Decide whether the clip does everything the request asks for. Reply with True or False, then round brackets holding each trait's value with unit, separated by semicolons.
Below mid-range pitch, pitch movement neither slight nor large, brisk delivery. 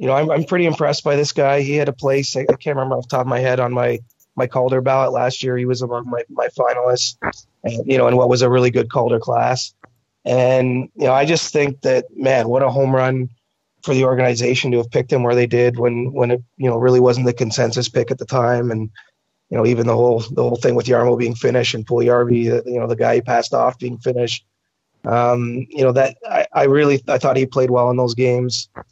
False (125 Hz; 1.4 semitones; 250 wpm)